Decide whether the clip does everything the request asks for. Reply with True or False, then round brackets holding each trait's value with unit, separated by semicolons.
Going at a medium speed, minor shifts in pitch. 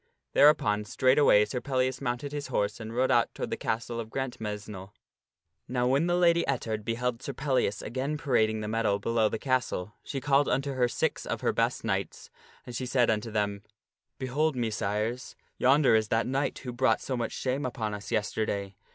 False (185 wpm; 3.6 semitones)